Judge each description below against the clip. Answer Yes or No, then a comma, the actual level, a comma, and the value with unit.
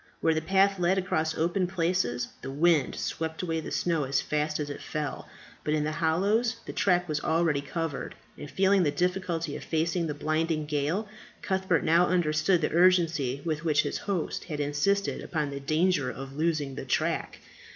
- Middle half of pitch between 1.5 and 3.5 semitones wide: Yes, average, 3.2 semitones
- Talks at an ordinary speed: Yes, average, 180 wpm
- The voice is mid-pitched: Yes, medium, 160 Hz